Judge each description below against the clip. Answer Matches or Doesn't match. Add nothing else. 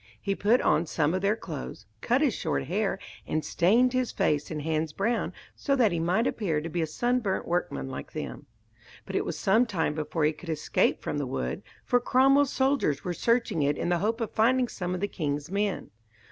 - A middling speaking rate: Doesn't match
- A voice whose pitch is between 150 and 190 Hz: Matches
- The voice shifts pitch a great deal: Matches